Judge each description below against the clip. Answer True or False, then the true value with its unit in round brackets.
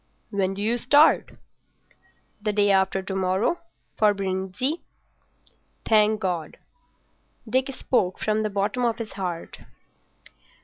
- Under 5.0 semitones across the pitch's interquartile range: True (3.1 semitones)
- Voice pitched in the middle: False (205 Hz)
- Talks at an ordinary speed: False (115 wpm)